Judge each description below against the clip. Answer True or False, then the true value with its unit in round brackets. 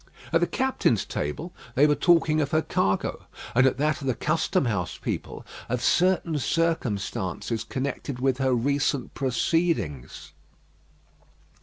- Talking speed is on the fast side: False (135 wpm)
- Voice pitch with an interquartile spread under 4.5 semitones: False (5.3 semitones)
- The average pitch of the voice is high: False (135 Hz)